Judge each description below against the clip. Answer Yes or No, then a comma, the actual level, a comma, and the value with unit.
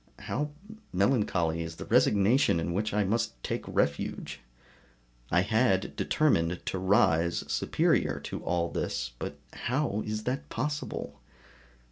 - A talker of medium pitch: No, low, 100 Hz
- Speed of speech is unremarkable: No, slow, 125 wpm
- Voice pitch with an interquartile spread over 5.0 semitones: Yes, wide, 5.6 semitones